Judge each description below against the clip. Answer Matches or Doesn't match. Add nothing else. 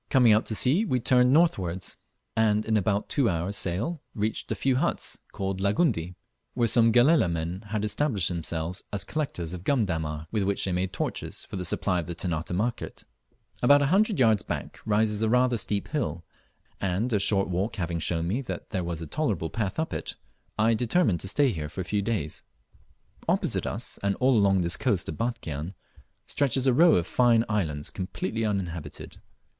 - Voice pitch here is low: Matches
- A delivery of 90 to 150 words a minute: Doesn't match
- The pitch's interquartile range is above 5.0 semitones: Matches